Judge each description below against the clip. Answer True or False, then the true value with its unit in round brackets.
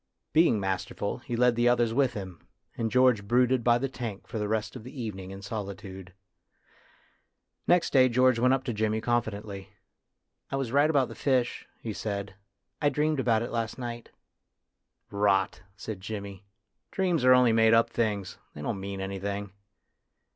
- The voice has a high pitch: False (115 Hz)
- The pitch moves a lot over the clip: False (3.9 semitones)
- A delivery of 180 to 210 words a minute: True (185 wpm)